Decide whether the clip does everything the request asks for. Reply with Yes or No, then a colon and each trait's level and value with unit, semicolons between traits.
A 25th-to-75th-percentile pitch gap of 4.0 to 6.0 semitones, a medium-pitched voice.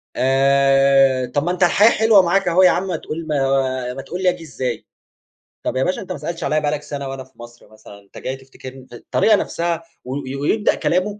Yes: average, 5.1 semitones; medium, 145 Hz